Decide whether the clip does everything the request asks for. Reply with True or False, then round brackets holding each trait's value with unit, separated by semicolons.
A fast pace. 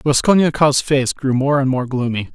False (180 wpm)